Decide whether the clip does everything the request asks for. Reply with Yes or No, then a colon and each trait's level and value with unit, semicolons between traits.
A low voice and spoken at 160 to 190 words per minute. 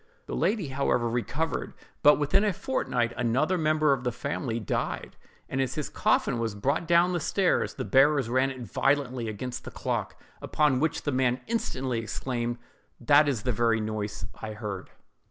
Yes: low, 130 Hz; average, 170 wpm